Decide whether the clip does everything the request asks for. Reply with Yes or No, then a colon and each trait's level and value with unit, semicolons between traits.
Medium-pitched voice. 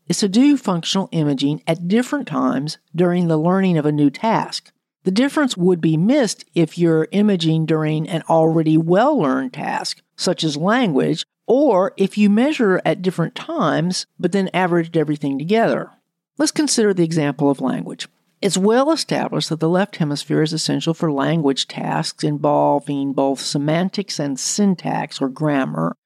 Yes: medium, 165 Hz